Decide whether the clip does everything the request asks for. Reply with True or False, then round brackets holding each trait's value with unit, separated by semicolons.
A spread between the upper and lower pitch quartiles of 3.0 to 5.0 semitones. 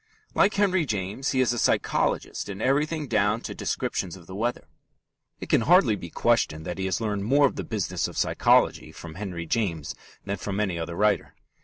False (5.4 semitones)